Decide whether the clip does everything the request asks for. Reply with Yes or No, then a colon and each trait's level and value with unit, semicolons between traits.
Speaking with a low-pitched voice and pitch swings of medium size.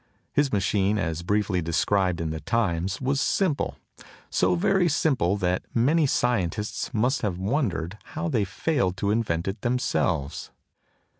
No: low, 100 Hz; wide, 6.0 semitones